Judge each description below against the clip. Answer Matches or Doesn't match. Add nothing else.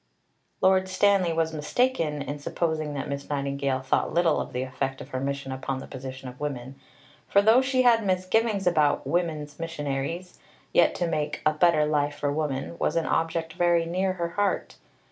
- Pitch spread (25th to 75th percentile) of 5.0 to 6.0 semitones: Doesn't match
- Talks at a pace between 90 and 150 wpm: Doesn't match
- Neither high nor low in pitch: Matches